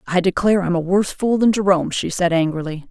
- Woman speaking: Yes, female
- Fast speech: Yes, fast, 225 wpm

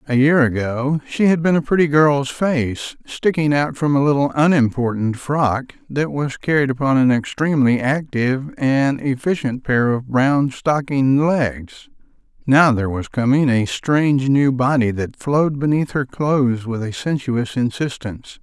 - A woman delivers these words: No, male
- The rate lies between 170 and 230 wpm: No, average, 155 wpm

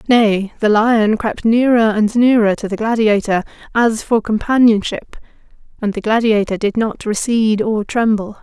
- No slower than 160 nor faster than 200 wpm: No, average, 150 wpm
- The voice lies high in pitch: Yes, high, 220 Hz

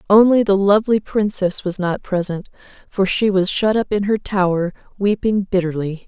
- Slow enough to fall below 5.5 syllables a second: Yes, 5.0 syllables/s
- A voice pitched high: Yes, high, 195 Hz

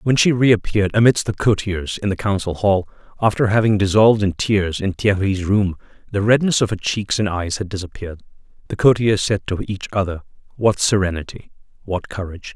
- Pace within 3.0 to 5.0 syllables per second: No, 5.6 syllables/s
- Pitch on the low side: Yes, low, 100 Hz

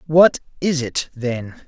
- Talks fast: No, average, 145 wpm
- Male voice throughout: Yes, male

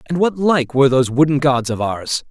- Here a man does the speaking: Yes, male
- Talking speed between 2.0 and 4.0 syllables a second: No, 5.8 syllables/s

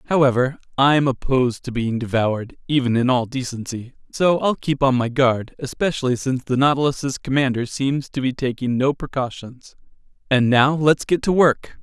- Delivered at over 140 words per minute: Yes, average, 165 wpm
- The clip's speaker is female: No, male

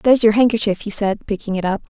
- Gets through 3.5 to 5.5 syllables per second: No, 6.8 syllables/s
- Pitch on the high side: Yes, high, 210 Hz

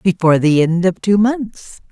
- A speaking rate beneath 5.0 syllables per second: Yes, 4.4 syllables/s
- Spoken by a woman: Yes, female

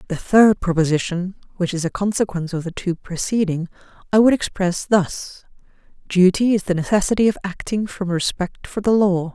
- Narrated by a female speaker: Yes, female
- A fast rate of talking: No, average, 165 wpm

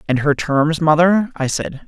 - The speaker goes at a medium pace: Yes, average, 190 wpm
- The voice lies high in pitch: No, medium, 160 Hz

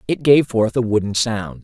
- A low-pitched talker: Yes, low, 115 Hz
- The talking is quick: Yes, fast, 220 wpm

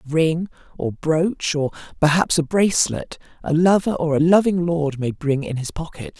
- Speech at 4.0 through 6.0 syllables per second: Yes, 4.8 syllables/s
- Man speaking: No, female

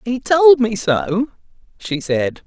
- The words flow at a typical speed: Yes, average, 145 wpm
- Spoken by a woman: No, male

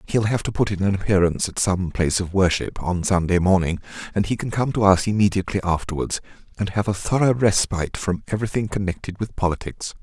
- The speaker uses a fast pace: No, average, 195 wpm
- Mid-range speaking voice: No, very low, 95 Hz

